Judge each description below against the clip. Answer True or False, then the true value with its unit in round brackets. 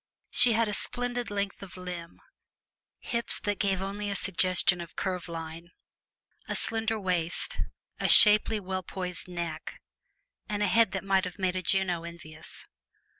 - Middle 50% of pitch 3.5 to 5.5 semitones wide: False (2.9 semitones)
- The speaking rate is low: False (155 wpm)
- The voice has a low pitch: False (190 Hz)